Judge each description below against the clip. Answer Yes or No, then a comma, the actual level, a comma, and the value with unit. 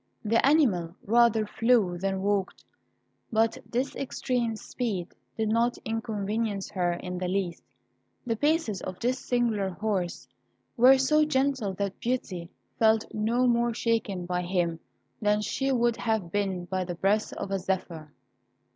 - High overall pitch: Yes, high, 215 Hz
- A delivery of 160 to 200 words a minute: No, average, 145 wpm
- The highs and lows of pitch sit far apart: No, average, 4.2 semitones